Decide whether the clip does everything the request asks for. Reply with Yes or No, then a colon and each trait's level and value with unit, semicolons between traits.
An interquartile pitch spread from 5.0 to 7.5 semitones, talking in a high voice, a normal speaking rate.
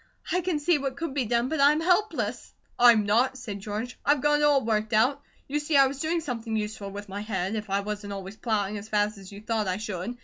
No: wide, 5.4 semitones; high, 225 Hz; fast, 245 wpm